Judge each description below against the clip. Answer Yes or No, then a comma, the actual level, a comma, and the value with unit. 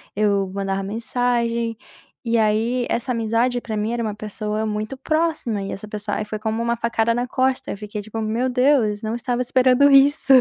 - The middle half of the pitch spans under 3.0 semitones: Yes, narrow, 2.6 semitones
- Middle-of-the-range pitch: No, high, 230 Hz